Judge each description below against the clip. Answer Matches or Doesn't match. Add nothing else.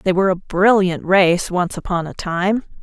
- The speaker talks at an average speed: Matches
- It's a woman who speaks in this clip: Matches